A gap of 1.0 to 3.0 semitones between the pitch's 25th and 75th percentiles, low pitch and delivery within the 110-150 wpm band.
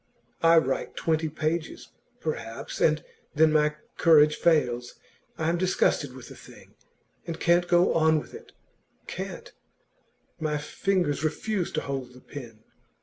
No: average, 2.7 semitones; medium, 155 Hz; average, 140 wpm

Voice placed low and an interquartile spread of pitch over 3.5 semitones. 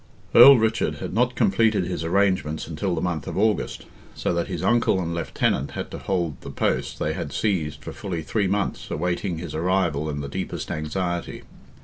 Yes: very low, 90 Hz; average, 4.1 semitones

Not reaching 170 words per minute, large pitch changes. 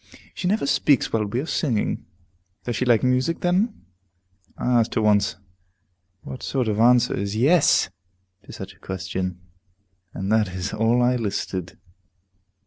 No: average, 155 wpm; average, 4.1 semitones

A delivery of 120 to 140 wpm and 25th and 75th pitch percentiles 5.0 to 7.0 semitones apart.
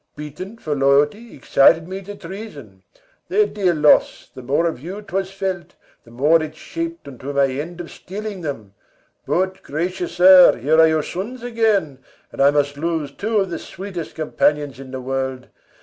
No: average, 175 wpm; average, 5.3 semitones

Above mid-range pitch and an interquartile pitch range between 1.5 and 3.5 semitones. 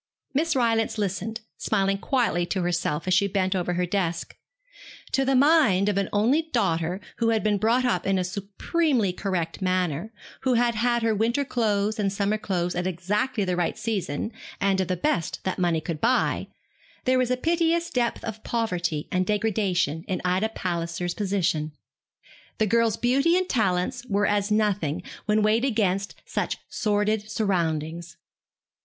No: high, 205 Hz; average, 4.1 semitones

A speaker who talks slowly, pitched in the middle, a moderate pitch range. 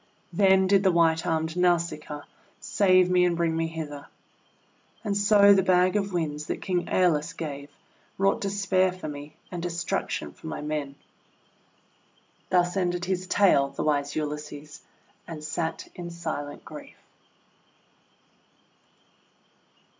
Yes: slow, 130 wpm; medium, 170 Hz; average, 3.4 semitones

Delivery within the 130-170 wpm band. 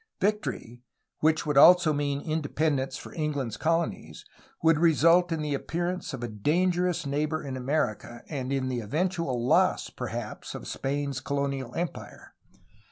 Yes: average, 145 wpm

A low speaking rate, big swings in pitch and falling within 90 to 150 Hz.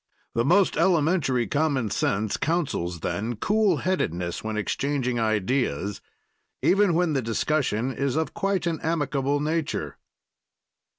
Yes: slow, 120 wpm; wide, 6.8 semitones; medium, 140 Hz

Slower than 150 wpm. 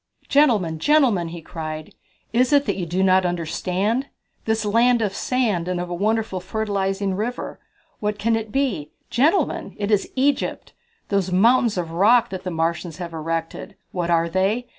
No: average, 165 wpm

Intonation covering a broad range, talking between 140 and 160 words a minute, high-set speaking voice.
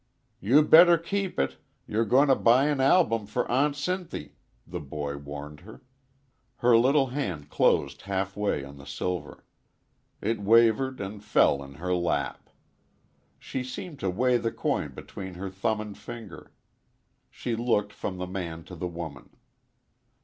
No: wide, 6.4 semitones; average, 155 wpm; low, 105 Hz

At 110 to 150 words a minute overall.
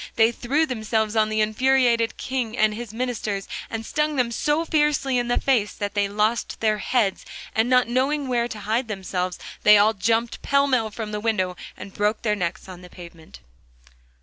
No: average, 190 wpm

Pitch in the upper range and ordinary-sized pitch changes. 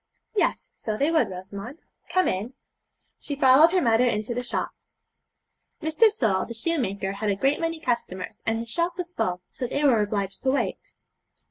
No: high, 245 Hz; wide, 7.3 semitones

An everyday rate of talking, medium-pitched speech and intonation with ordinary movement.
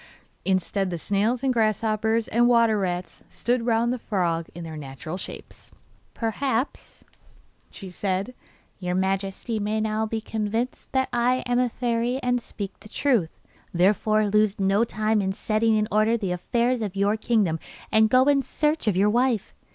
No: average, 165 wpm; high, 215 Hz; average, 3.4 semitones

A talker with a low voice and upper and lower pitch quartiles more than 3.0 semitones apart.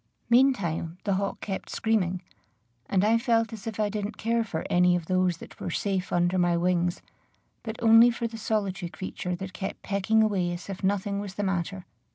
No: high, 195 Hz; average, 3.6 semitones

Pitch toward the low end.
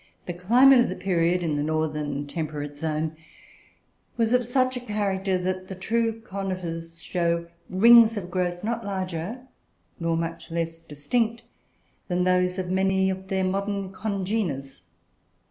No: medium, 185 Hz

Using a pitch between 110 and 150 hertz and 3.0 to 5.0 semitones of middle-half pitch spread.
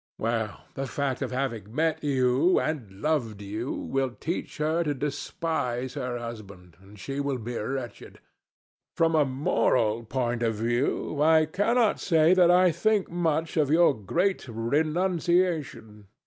No: low, 135 Hz; wide, 5.6 semitones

